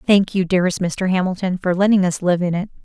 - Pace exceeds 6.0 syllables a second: Yes, 6.2 syllables/s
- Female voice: Yes, female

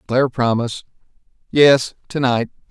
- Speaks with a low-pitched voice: Yes, low, 125 Hz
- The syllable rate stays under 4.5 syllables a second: No, 5.1 syllables/s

